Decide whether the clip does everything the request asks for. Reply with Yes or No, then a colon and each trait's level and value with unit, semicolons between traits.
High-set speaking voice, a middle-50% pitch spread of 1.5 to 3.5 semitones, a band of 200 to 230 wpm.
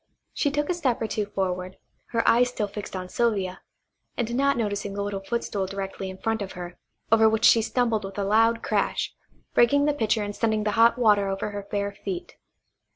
Yes: high, 215 Hz; average, 3.0 semitones; fast, 205 wpm